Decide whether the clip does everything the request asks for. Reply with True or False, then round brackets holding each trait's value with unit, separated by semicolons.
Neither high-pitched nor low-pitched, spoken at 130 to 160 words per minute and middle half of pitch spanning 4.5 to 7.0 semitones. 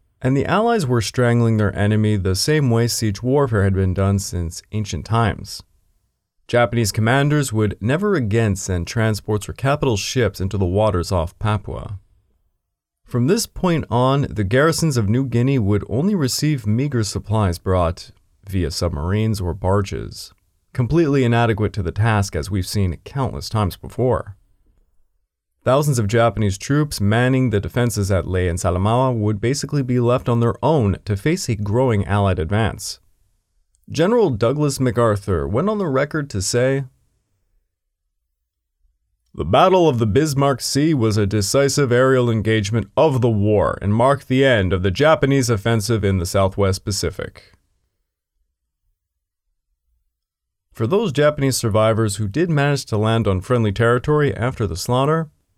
False (105 Hz; 150 wpm; 5.2 semitones)